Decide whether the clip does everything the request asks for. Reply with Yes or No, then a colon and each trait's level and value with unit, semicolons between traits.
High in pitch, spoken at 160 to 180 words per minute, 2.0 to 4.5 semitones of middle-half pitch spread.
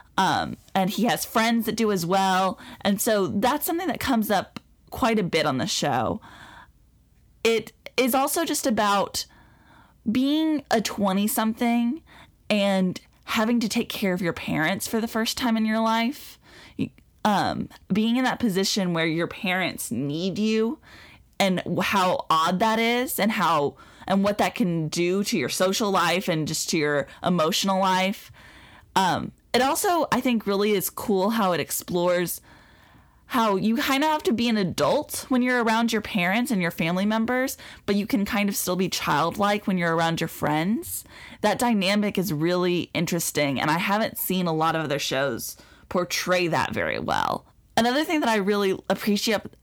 Yes: high, 205 Hz; average, 175 wpm; average, 4.2 semitones